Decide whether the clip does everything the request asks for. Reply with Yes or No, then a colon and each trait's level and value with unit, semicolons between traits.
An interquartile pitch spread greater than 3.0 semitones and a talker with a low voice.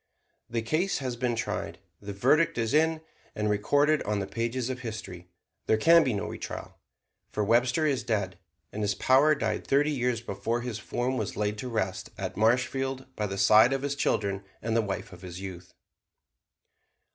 Yes: average, 4.2 semitones; low, 115 Hz